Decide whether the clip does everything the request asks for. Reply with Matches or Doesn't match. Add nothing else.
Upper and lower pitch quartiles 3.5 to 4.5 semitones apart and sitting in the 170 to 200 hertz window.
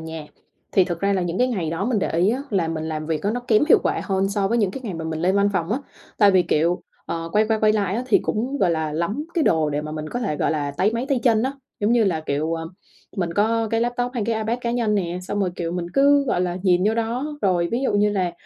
Doesn't match